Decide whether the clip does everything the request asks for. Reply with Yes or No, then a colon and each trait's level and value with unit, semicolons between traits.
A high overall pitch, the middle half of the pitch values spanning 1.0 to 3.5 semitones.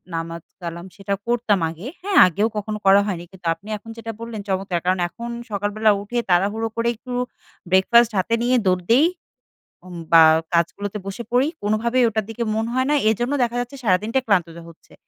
No: high, 210 Hz; average, 4.1 semitones